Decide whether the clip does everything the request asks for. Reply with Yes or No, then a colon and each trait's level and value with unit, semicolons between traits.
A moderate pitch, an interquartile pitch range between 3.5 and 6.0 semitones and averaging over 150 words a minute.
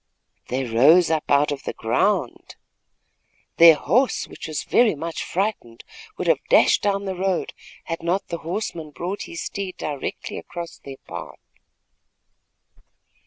No: medium, 170 Hz; average, 4.5 semitones; average, 140 wpm